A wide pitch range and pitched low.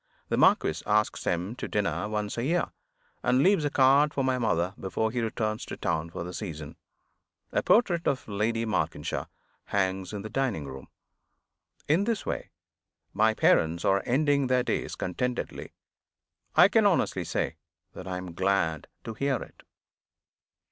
Yes: wide, 6.0 semitones; low, 110 Hz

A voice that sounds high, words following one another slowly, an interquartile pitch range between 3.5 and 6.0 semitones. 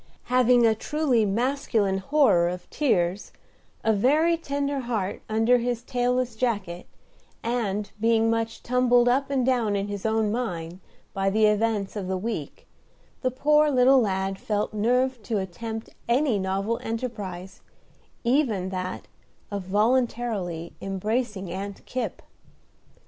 Yes: high, 225 Hz; slow, 130 wpm; average, 4.3 semitones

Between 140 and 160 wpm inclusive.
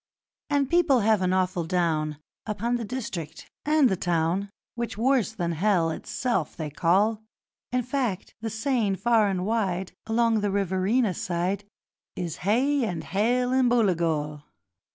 Yes: average, 145 wpm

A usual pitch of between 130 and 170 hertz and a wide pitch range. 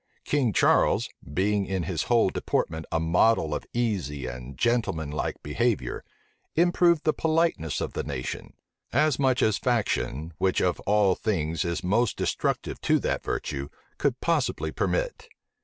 No: low, 100 Hz; wide, 7.5 semitones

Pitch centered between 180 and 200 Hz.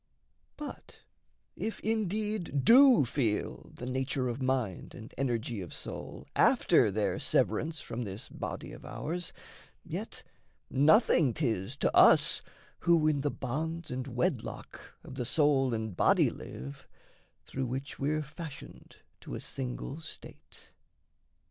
No: low, 135 Hz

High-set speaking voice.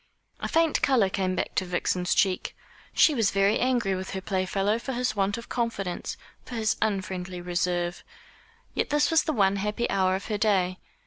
Yes: high, 195 Hz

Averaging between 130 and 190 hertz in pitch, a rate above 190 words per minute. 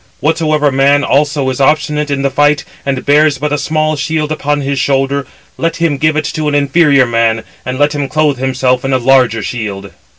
Yes: medium, 140 Hz; average, 200 wpm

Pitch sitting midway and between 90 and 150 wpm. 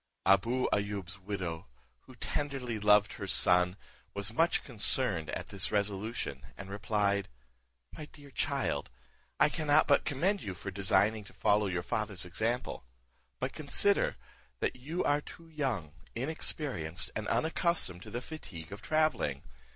No: low, 105 Hz; average, 140 wpm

